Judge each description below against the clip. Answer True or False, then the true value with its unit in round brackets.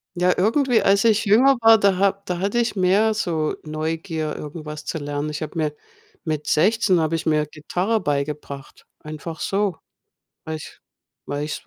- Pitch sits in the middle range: True (165 Hz)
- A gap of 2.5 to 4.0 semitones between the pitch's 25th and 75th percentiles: False (4.8 semitones)